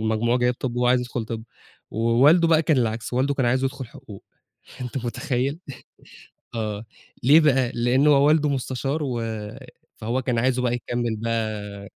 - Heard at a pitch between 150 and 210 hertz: No, low, 125 Hz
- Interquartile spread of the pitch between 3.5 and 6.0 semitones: No, average, 2.8 semitones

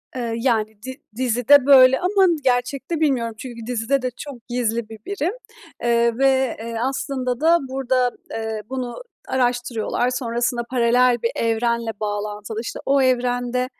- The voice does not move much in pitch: Yes, narrow, 2.1 semitones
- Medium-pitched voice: No, high, 245 Hz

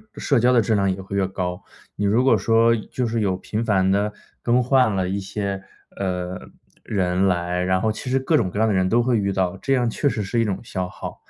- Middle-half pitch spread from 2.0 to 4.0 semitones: Yes, average, 3.7 semitones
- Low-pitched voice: Yes, low, 100 Hz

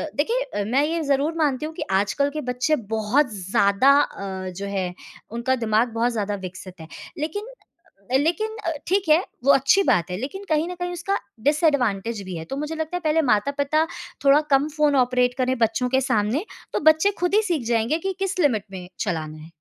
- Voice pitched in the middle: No, very high, 270 Hz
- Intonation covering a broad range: Yes, wide, 6.7 semitones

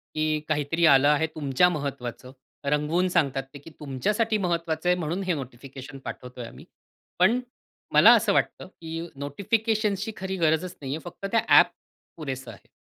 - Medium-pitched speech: Yes, medium, 155 Hz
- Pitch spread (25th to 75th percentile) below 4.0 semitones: No, average, 4.5 semitones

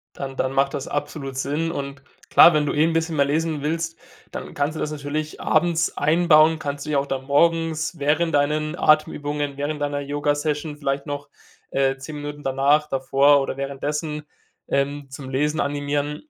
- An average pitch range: No, narrow, 1.6 semitones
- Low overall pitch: No, medium, 145 Hz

